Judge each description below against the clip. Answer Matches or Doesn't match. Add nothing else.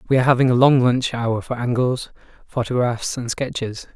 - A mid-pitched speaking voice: Doesn't match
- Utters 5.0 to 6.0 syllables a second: Matches